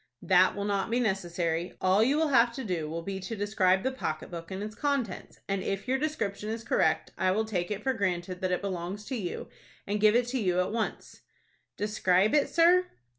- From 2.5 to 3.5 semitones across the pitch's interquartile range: No, average, 4.1 semitones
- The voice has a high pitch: Yes, high, 200 Hz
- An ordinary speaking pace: No, fast, 220 wpm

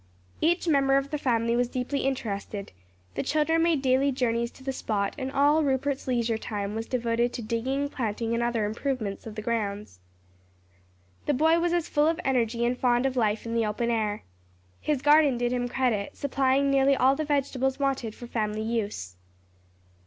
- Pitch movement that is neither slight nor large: Yes, average, 3.4 semitones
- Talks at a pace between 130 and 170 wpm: No, average, 180 wpm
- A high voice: Yes, very high, 250 Hz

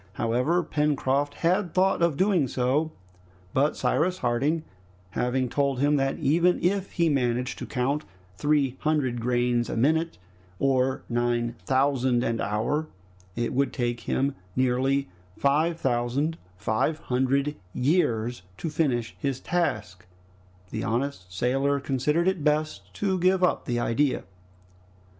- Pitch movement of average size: Yes, average, 4.1 semitones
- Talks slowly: Yes, slow, 130 wpm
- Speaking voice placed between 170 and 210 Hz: No, low, 135 Hz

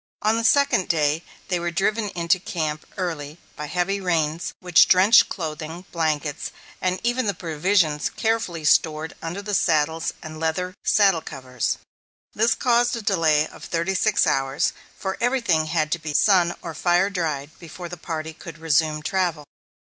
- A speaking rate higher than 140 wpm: Yes, average, 160 wpm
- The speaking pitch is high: No, medium, 170 Hz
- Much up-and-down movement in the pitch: No, average, 3.7 semitones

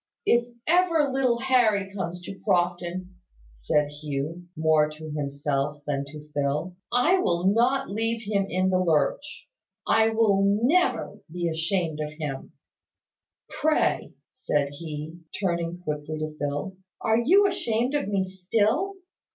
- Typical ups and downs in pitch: No, wide, 7.0 semitones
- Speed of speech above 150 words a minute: No, slow, 135 wpm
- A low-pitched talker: No, medium, 180 Hz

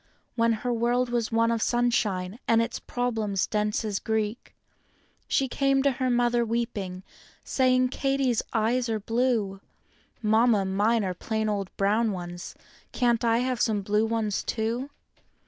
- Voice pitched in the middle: No, high, 230 Hz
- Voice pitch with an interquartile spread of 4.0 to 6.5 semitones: No, narrow, 2.5 semitones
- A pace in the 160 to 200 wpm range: No, average, 145 wpm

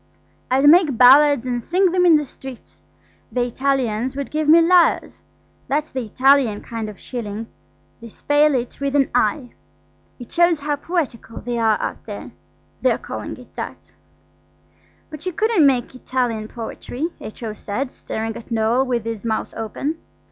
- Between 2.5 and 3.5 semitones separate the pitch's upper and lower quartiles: No, average, 4.5 semitones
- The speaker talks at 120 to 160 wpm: Yes, average, 155 wpm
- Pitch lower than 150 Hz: No, very high, 260 Hz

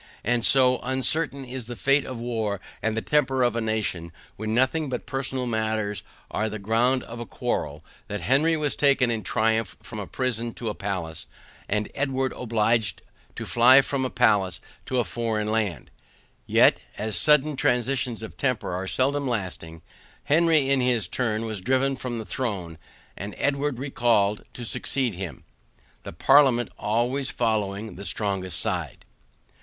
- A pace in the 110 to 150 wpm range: No, average, 160 wpm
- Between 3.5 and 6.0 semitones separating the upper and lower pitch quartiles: Yes, average, 3.8 semitones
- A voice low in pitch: Yes, low, 115 Hz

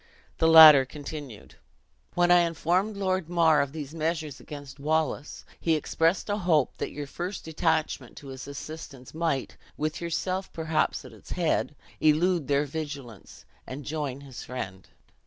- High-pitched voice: No, medium, 155 Hz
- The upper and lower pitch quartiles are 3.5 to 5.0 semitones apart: No, average, 2.9 semitones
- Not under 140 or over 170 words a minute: Yes, average, 150 wpm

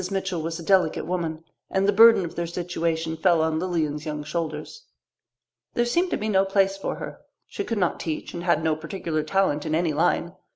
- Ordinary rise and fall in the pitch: Yes, average, 3.3 semitones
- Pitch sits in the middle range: Yes, medium, 170 Hz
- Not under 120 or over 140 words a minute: No, fast, 205 wpm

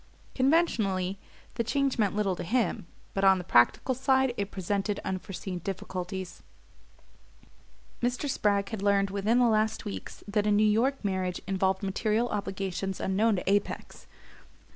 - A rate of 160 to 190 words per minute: No, average, 140 wpm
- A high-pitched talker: Yes, high, 200 Hz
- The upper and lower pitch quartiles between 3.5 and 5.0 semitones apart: No, average, 3.0 semitones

